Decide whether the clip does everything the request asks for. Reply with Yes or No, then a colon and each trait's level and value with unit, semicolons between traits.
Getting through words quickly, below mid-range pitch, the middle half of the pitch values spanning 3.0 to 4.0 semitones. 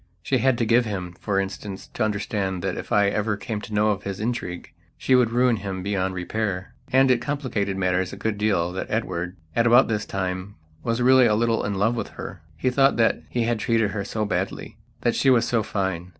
Yes: fast, 220 wpm; low, 105 Hz; average, 3.5 semitones